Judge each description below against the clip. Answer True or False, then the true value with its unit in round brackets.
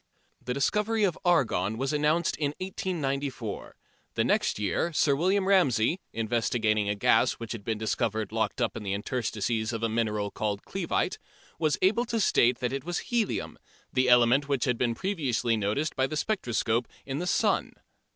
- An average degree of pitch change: False (6.5 semitones)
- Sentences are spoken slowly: False (170 wpm)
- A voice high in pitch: False (125 Hz)